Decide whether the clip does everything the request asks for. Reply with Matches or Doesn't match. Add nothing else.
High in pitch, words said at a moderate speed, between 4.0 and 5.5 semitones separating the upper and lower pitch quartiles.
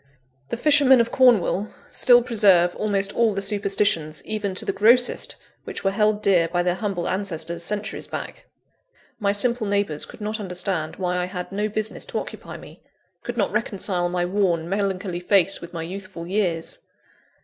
Doesn't match